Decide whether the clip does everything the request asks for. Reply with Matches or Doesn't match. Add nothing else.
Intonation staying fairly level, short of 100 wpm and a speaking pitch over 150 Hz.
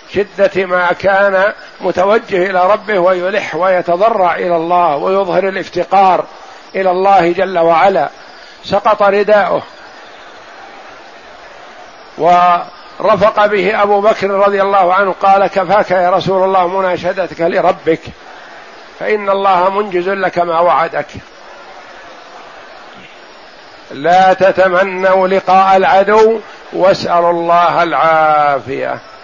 Matches